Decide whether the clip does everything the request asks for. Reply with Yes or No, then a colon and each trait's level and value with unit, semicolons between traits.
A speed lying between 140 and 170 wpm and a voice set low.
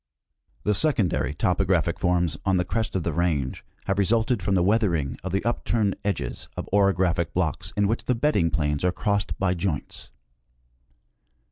Yes: average, 160 wpm; very low, 95 Hz